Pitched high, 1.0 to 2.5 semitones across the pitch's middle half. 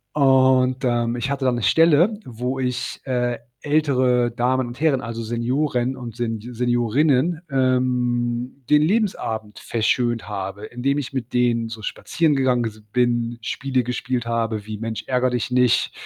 No: low, 125 Hz; narrow, 2.1 semitones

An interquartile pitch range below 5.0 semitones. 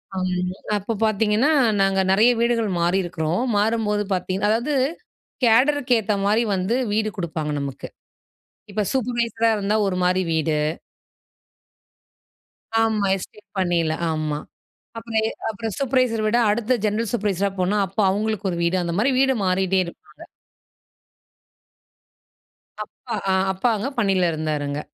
Yes: average, 3.8 semitones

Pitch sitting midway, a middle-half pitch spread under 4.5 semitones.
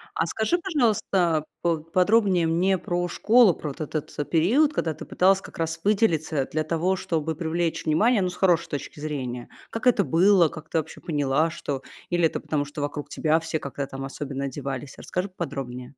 Yes: medium, 165 Hz; average, 4.1 semitones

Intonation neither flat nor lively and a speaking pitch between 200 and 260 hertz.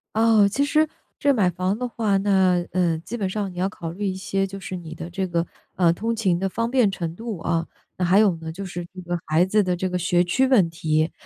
No: average, 3.3 semitones; medium, 185 Hz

